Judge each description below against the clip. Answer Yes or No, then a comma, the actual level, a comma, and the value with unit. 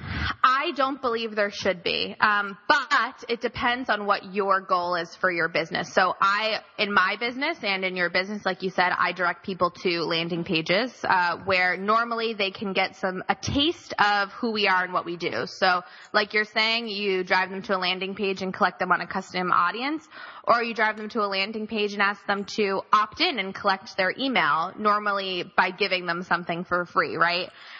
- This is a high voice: Yes, high, 200 Hz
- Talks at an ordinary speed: No, fast, 210 wpm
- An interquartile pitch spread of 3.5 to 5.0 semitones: No, average, 2.9 semitones